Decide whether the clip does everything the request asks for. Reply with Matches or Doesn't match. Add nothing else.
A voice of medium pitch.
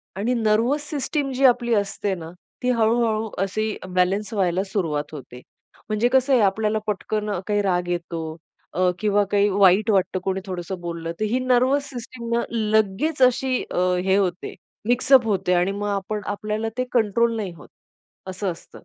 Doesn't match